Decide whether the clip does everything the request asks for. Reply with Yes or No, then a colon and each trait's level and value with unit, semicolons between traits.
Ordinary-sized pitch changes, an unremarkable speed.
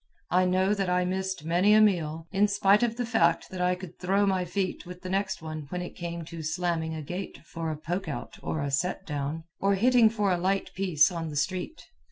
No: average, 3.0 semitones; fast, 235 wpm